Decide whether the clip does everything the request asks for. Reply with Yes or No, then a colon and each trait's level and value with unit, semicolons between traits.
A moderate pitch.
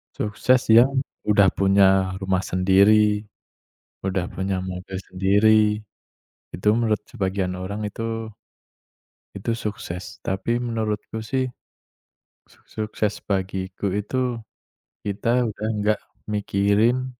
No: low, 105 Hz